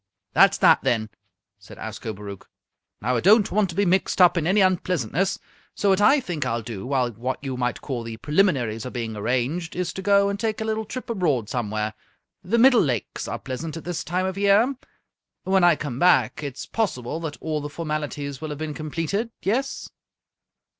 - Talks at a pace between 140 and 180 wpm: No, average, 195 wpm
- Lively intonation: Yes, wide, 7.7 semitones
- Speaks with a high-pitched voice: No, medium, 155 Hz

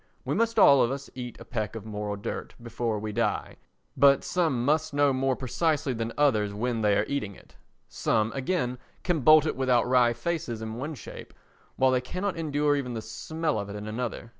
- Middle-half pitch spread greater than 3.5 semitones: Yes, average, 4.6 semitones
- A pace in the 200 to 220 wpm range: Yes, fast, 205 wpm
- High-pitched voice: No, low, 125 Hz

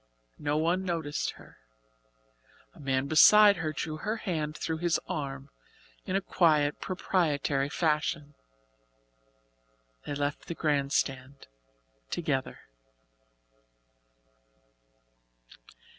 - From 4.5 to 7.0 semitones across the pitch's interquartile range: No, average, 3.2 semitones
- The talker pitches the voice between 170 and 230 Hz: No, medium, 150 Hz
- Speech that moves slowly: Yes, slow, 95 wpm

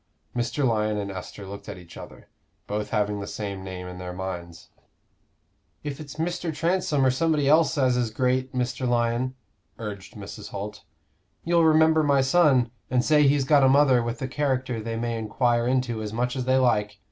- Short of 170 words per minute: No, average, 185 wpm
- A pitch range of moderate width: Yes, average, 4.9 semitones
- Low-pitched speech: Yes, low, 125 Hz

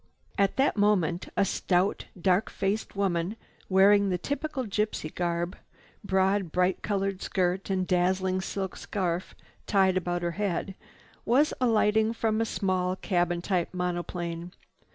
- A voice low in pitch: No, high, 190 Hz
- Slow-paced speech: Yes, slow, 130 wpm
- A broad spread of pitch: No, narrow, 2.4 semitones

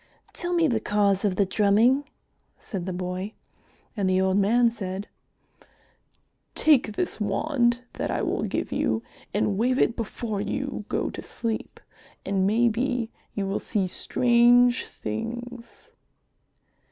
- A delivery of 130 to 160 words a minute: Yes, slow, 135 wpm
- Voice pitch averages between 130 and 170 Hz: No, high, 220 Hz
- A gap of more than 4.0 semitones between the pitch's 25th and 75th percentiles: No, average, 3.6 semitones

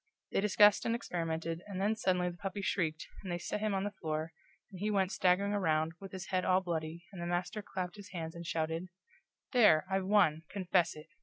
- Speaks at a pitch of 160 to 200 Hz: Yes, medium, 185 Hz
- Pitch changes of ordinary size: Yes, average, 3.3 semitones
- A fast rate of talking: Yes, fast, 215 wpm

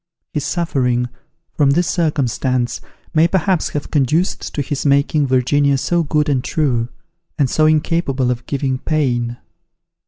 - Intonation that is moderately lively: Yes, average, 3.4 semitones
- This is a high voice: No, medium, 140 Hz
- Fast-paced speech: No, slow, 135 wpm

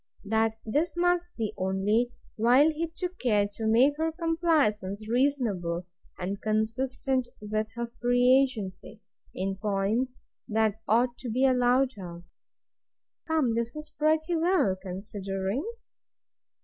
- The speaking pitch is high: Yes, high, 235 Hz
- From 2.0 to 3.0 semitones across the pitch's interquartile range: No, average, 5.1 semitones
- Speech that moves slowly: Yes, slow, 125 wpm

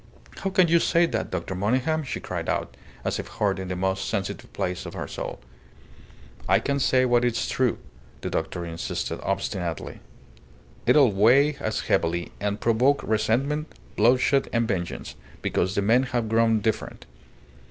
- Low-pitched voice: Yes, low, 115 Hz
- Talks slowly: No, average, 160 wpm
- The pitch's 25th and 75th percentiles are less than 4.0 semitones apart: No, average, 5.2 semitones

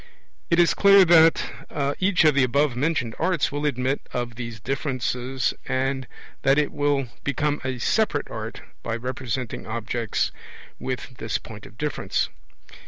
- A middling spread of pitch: Yes, average, 3.6 semitones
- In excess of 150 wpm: No, average, 145 wpm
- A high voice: No, low, 135 Hz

